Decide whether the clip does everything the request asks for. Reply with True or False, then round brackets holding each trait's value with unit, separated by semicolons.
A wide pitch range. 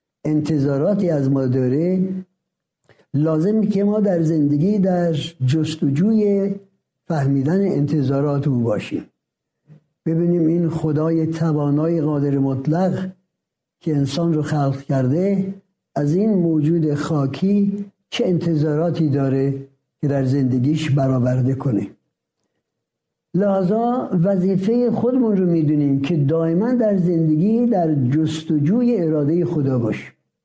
False (4.5 semitones)